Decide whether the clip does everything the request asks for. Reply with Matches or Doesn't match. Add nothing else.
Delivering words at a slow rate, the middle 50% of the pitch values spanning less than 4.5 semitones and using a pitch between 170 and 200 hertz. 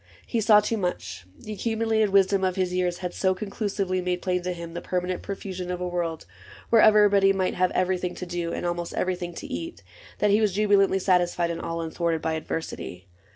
Doesn't match